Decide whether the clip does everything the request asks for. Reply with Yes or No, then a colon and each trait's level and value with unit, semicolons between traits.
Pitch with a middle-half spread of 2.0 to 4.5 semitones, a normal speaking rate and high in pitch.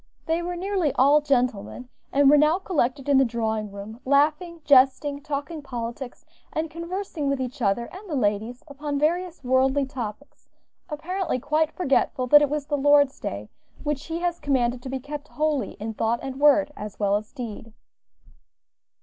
Yes: average, 3.5 semitones; average, 170 wpm; very high, 280 Hz